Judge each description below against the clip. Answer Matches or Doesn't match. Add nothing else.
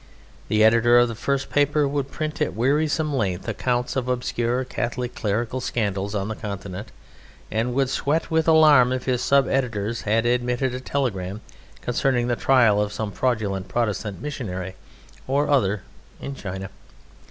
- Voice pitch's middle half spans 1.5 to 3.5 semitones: Doesn't match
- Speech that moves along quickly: Doesn't match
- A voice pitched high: Doesn't match